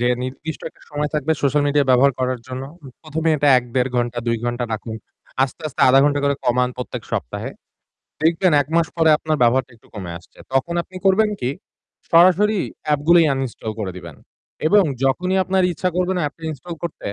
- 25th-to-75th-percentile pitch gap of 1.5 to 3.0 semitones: No, average, 5.0 semitones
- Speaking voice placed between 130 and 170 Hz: Yes, medium, 140 Hz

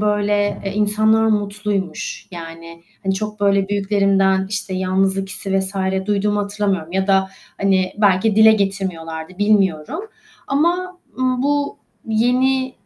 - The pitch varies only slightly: Yes, narrow, 2.0 semitones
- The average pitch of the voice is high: Yes, high, 200 Hz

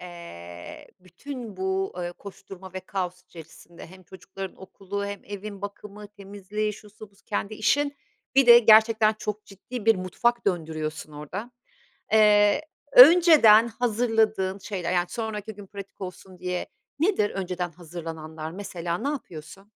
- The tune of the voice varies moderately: Yes, average, 3.2 semitones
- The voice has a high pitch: Yes, high, 200 Hz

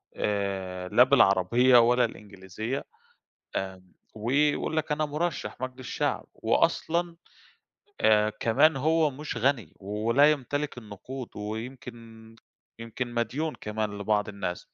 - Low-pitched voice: Yes, low, 115 Hz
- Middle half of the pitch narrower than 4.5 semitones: No, average, 4.8 semitones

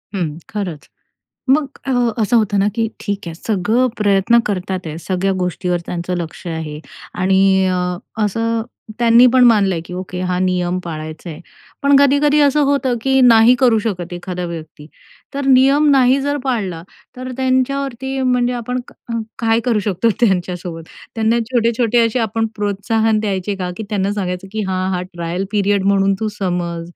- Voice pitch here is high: Yes, high, 205 Hz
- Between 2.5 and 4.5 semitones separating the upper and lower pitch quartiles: No, average, 5.1 semitones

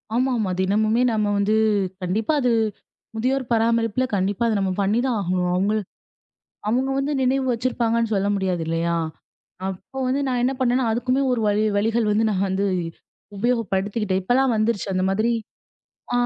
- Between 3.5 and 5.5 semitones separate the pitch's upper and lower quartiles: Yes, average, 3.8 semitones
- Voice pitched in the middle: No, high, 220 Hz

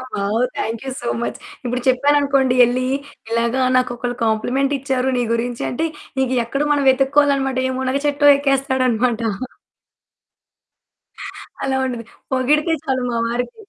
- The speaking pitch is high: Yes, very high, 255 Hz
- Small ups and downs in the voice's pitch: Yes, narrow, 2.2 semitones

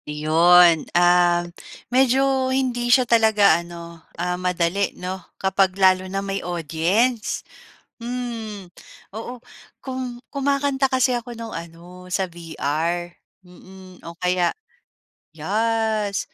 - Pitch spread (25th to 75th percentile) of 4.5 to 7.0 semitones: Yes, wide, 5.4 semitones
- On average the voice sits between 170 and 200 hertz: Yes, high, 190 Hz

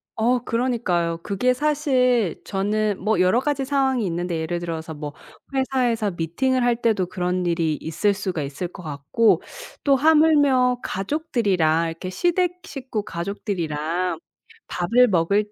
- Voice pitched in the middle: No, high, 205 Hz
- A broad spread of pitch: Yes, wide, 6.6 semitones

